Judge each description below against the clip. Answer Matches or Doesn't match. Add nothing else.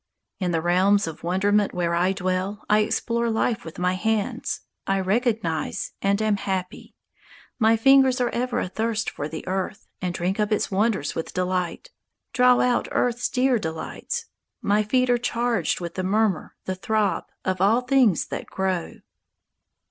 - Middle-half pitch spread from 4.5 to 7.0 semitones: Doesn't match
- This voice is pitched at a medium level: Doesn't match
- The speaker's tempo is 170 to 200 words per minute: Doesn't match